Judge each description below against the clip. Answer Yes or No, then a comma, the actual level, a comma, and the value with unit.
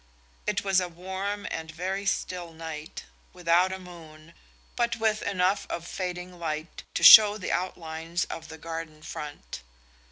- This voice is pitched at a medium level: Yes, medium, 175 Hz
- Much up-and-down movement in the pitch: No, average, 2.7 semitones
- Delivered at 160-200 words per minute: No, average, 150 wpm